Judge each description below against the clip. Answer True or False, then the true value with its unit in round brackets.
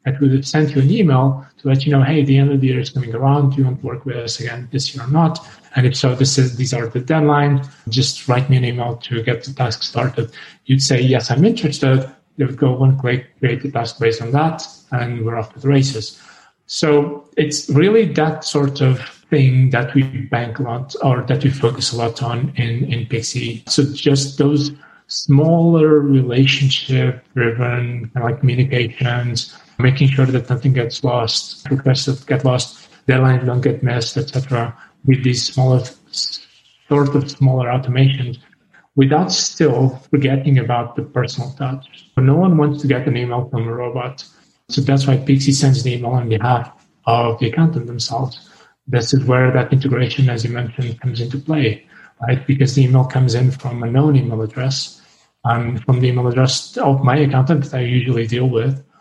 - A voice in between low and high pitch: False (130 Hz)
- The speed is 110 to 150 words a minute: False (195 wpm)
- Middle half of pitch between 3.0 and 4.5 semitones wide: False (2.4 semitones)